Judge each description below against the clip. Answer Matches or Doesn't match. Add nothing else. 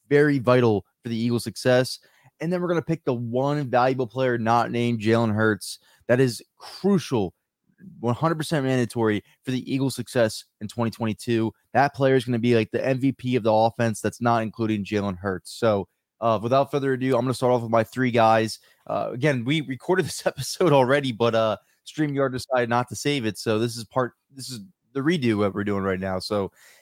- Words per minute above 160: Matches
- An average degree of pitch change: Matches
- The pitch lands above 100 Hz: Matches